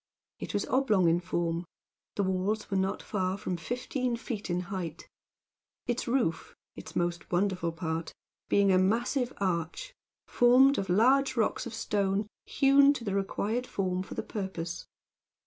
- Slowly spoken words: No, average, 150 wpm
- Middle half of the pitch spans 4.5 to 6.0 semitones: Yes, average, 5.1 semitones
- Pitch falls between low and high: No, high, 195 Hz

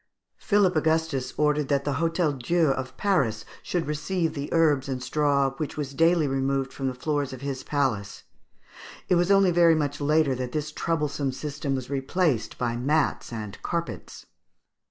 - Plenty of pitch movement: No, average, 3.2 semitones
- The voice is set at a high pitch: No, medium, 145 Hz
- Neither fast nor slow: Yes, average, 165 wpm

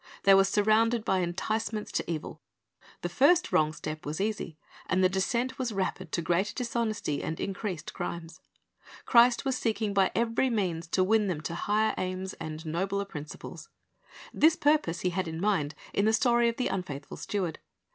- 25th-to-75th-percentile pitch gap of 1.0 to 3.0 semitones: No, average, 4.7 semitones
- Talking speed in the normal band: Yes, average, 175 wpm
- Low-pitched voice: No, high, 195 Hz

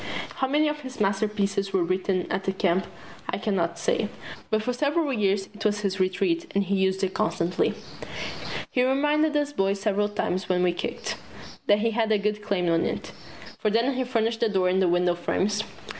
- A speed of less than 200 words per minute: No, fast, 205 wpm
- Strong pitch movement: No, average, 3.7 semitones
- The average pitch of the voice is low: No, high, 205 Hz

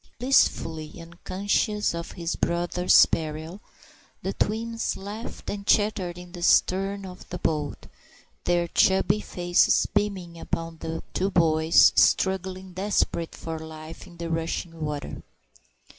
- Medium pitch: Yes, medium, 175 Hz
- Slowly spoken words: Yes, slow, 125 wpm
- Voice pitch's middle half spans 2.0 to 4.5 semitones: Yes, average, 2.9 semitones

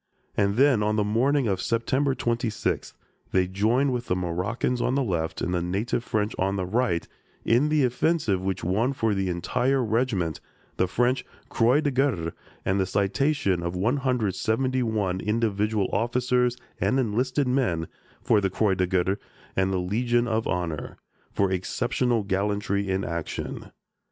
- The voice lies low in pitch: Yes, low, 105 Hz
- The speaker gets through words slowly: No, average, 150 wpm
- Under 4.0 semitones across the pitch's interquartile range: No, average, 4.9 semitones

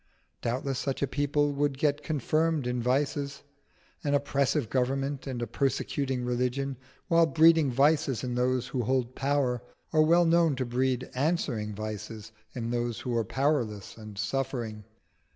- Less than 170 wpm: Yes, average, 150 wpm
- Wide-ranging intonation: No, average, 3.1 semitones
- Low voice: Yes, low, 130 Hz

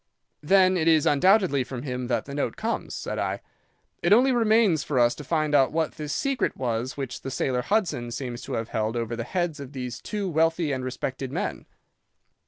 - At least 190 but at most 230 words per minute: Yes, average, 200 wpm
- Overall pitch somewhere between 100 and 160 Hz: Yes, medium, 140 Hz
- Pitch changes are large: Yes, wide, 5.7 semitones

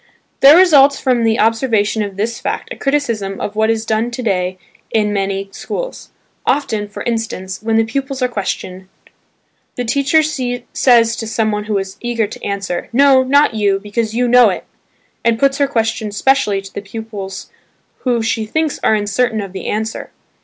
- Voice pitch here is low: No, high, 225 Hz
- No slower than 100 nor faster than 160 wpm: No, average, 175 wpm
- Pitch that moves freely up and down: No, average, 3.5 semitones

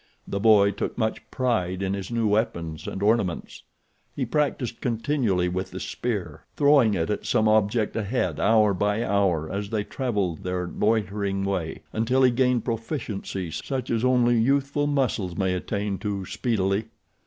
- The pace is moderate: Yes, average, 160 wpm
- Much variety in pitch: No, average, 3.7 semitones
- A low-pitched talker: Yes, low, 105 Hz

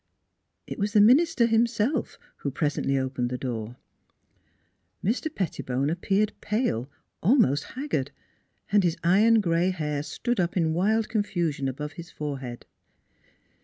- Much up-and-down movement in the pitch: Yes, wide, 7.6 semitones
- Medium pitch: Yes, medium, 175 Hz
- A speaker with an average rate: No, slow, 130 wpm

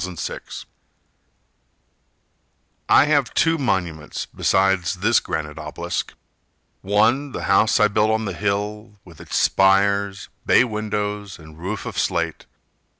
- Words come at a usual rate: No, slow, 125 wpm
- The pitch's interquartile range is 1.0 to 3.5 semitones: Yes, average, 2.9 semitones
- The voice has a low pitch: Yes, low, 100 Hz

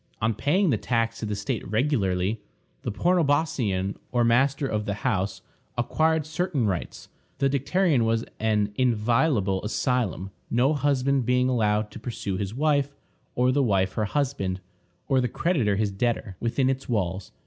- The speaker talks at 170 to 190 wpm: No, average, 155 wpm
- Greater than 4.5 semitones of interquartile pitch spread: Yes, average, 4.9 semitones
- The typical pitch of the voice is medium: No, low, 120 Hz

